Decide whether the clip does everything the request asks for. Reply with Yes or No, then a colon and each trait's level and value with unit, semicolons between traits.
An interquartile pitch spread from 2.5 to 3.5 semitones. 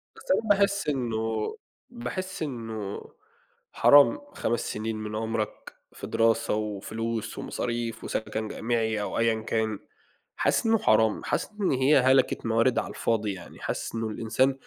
Yes: average, 2.8 semitones